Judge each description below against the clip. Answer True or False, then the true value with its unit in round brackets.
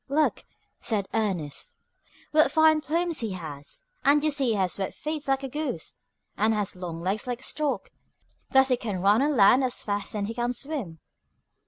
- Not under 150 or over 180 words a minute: False (190 wpm)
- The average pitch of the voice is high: True (240 Hz)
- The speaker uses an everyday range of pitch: False (6.7 semitones)